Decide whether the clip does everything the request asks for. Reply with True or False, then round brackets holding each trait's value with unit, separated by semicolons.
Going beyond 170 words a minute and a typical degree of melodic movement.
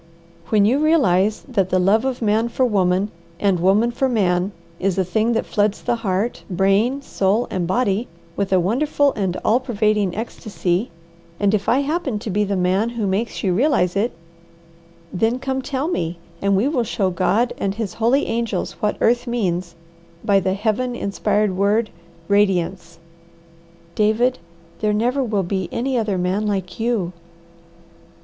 False (165 wpm; 3.8 semitones)